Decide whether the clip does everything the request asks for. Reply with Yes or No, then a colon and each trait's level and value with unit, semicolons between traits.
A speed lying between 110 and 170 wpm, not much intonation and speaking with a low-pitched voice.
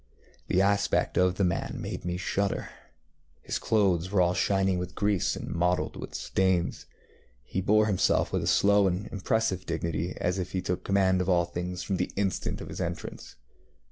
No: average, 180 wpm; narrow, 1.9 semitones; very low, 95 Hz